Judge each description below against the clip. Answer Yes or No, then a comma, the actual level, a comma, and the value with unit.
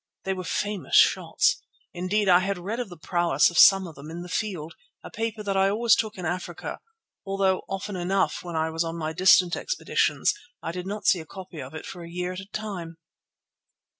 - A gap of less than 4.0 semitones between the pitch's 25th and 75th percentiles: Yes, narrow, 2.6 semitones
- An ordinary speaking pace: No, fast, 215 wpm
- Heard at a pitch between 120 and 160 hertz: No, medium, 185 Hz